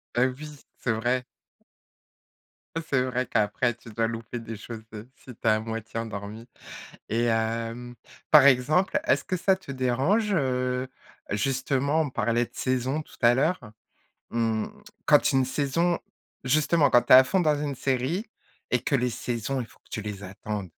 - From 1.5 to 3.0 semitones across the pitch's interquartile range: No, average, 3.5 semitones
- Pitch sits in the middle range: No, low, 125 Hz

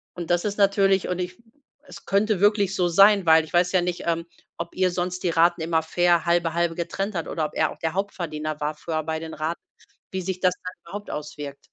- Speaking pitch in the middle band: Yes, medium, 175 Hz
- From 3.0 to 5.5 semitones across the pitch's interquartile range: No, narrow, 2.6 semitones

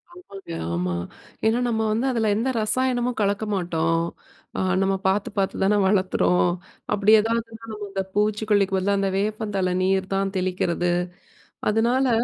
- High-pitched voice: Yes, high, 205 Hz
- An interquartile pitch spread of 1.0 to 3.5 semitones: Yes, average, 2.7 semitones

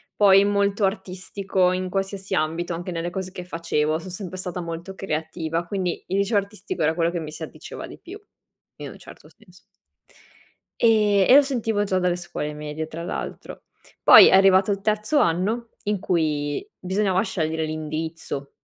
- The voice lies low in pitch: No, medium, 185 Hz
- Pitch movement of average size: Yes, average, 3.3 semitones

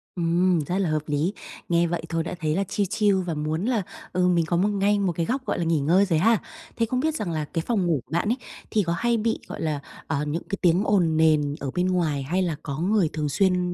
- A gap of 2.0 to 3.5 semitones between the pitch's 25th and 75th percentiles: No, average, 3.9 semitones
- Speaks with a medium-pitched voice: Yes, medium, 175 Hz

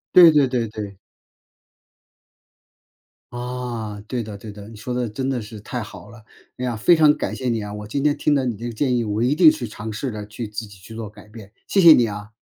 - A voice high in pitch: No, low, 115 Hz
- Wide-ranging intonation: No, average, 3.2 semitones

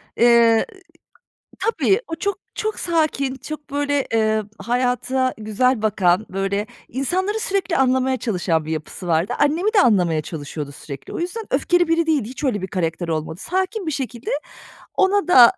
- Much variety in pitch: Yes, wide, 8.9 semitones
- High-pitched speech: Yes, very high, 255 Hz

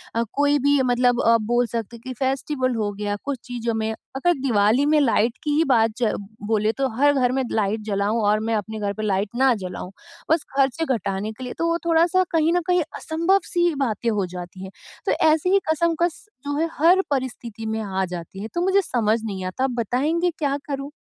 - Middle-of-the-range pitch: No, high, 245 Hz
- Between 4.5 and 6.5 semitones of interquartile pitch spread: Yes, wide, 5.5 semitones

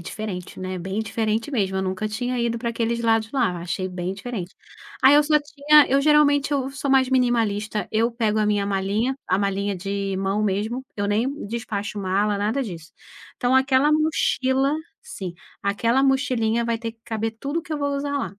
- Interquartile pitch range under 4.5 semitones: No, average, 4.8 semitones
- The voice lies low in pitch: No, high, 225 Hz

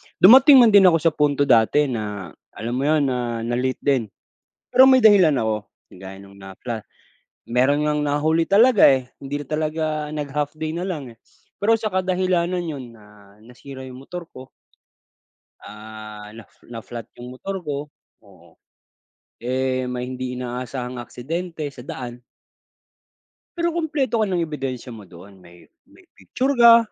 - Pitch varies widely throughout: Yes, wide, 6.5 semitones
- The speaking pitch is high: No, low, 135 Hz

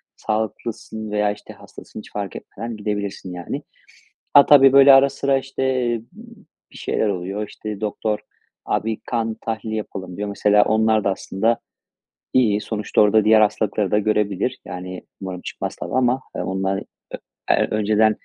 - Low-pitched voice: Yes, low, 105 Hz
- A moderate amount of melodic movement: No, narrow, 2.0 semitones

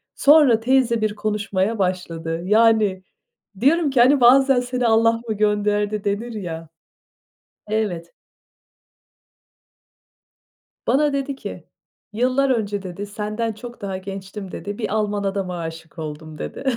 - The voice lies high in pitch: Yes, high, 210 Hz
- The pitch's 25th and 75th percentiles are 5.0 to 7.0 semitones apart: No, average, 3.8 semitones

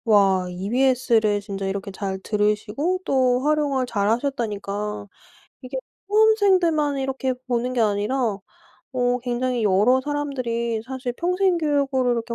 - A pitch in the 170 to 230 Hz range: No, very high, 250 Hz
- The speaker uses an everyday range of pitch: Yes, average, 4.8 semitones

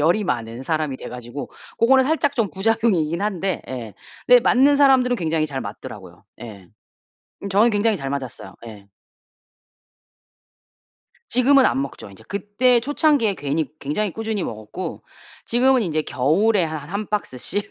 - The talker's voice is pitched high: Yes, high, 195 Hz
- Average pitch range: No, wide, 8.8 semitones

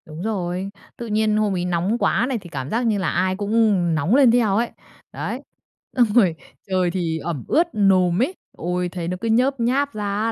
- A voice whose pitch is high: Yes, high, 200 Hz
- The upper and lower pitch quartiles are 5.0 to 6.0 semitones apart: No, average, 4.4 semitones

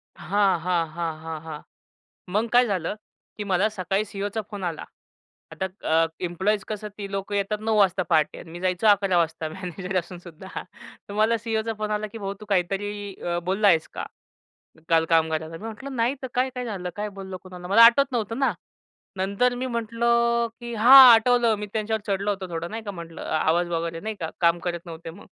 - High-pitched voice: Yes, high, 200 Hz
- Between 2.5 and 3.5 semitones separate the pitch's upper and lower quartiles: No, average, 4.1 semitones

